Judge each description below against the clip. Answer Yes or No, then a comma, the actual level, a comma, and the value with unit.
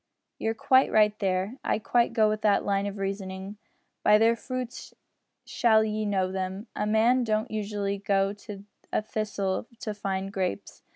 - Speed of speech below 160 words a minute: No, average, 165 wpm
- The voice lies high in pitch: Yes, high, 210 Hz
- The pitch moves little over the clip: Yes, narrow, 1.8 semitones